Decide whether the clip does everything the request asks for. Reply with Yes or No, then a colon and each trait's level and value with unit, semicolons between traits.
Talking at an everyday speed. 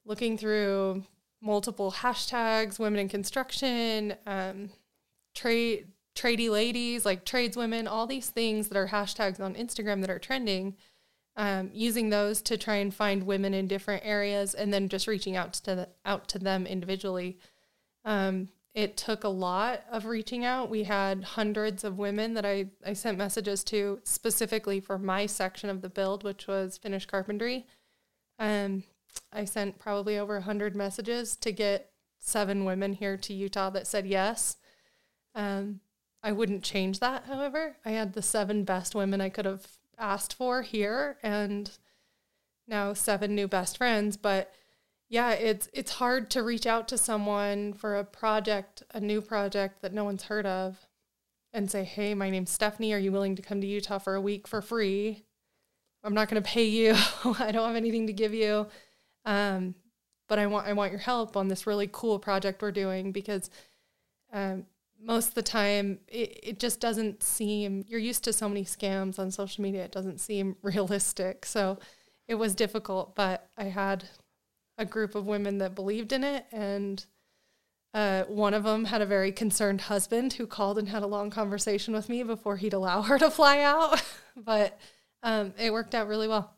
Yes: average, 180 wpm